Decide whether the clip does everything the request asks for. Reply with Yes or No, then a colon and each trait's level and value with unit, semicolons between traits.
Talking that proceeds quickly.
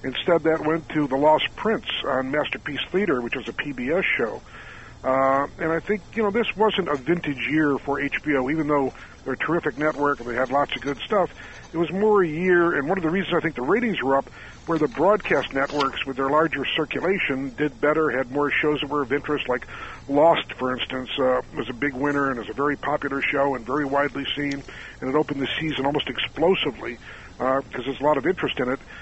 Yes: fast, 225 wpm